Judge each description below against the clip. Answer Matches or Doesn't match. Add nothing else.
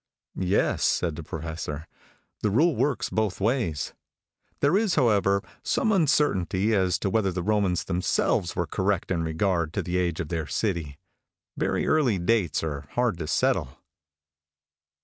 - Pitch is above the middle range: Doesn't match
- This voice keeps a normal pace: Matches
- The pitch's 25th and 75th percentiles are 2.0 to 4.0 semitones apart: Doesn't match